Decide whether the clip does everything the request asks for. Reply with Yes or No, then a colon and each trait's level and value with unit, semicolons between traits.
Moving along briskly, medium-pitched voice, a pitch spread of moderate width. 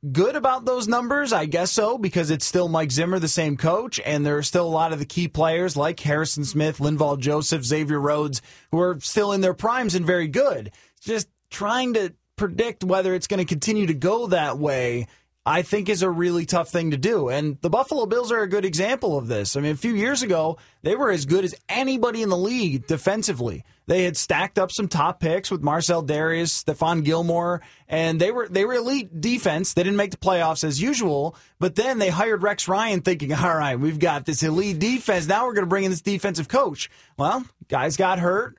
Yes: fast, 220 wpm; medium, 180 Hz; average, 4.4 semitones